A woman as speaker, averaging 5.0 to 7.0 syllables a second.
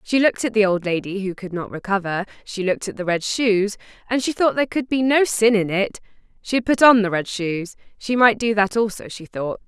Yes: female; 5.5 syllables/s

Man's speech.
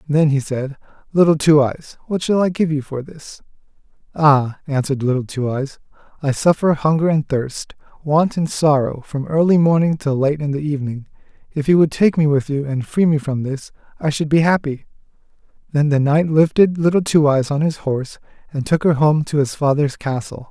Yes: male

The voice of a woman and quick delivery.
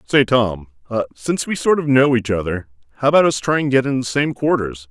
No: male; fast, 230 wpm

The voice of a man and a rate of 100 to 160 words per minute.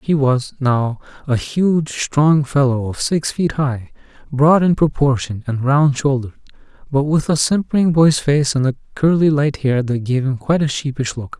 No: male; average, 180 wpm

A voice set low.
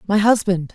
No: high, 195 Hz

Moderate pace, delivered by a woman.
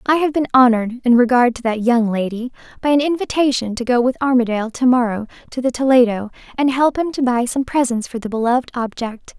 No: fast, 210 wpm; female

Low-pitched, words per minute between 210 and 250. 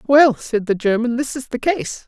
No: very high, 250 Hz; fast, 230 wpm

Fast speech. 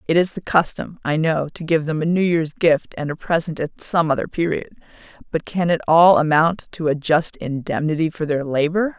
Yes: fast, 215 wpm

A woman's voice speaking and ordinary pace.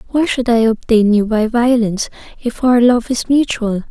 Yes: female; average, 185 wpm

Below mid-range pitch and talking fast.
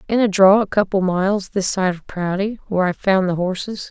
No: high, 195 Hz; fast, 245 wpm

